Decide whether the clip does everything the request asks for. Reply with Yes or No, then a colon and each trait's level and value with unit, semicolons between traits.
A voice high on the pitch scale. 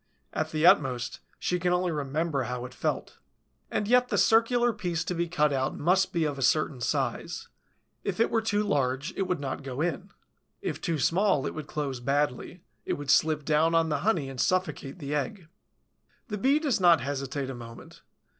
No: medium, 155 Hz